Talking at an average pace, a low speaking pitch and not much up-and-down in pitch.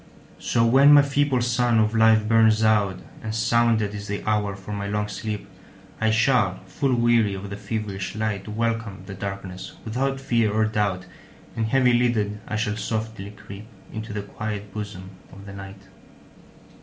Yes: average, 150 wpm; low, 110 Hz; narrow, 2.3 semitones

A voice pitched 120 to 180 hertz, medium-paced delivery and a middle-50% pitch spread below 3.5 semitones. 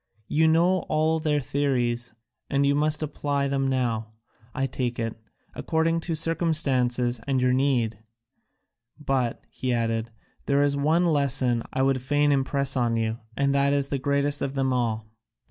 Yes: low, 135 Hz; average, 165 wpm; average, 2.9 semitones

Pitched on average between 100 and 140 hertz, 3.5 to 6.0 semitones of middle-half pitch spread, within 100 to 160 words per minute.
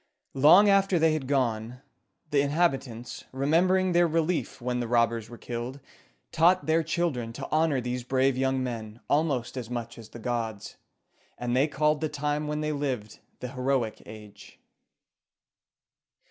Yes: low, 135 Hz; average, 4.6 semitones; average, 150 wpm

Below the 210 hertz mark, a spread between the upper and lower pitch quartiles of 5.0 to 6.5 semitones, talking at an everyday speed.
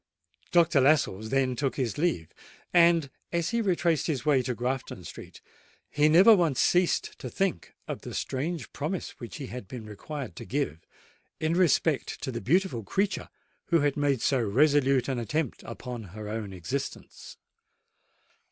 Yes: medium, 140 Hz; wide, 5.6 semitones; average, 160 wpm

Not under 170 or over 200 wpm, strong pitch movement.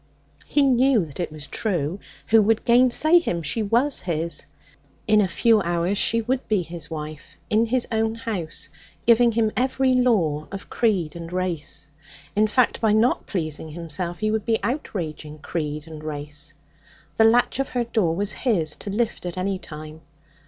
Yes: average, 175 wpm; wide, 6.0 semitones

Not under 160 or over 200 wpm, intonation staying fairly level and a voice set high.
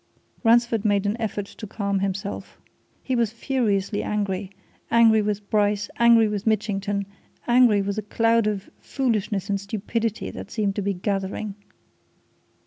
No: average, 140 wpm; narrow, 2.2 semitones; high, 210 Hz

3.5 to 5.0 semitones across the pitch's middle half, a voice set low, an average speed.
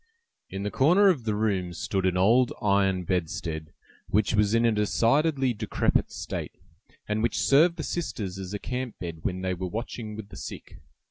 Yes: average, 4.5 semitones; low, 105 Hz; average, 185 wpm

